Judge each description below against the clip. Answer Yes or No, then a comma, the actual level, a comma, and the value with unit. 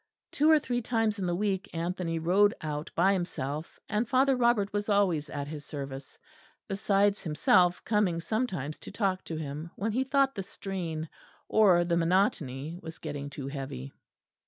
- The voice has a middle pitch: Yes, medium, 180 Hz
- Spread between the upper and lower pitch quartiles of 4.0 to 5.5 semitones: Yes, average, 5.0 semitones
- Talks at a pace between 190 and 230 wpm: No, average, 165 wpm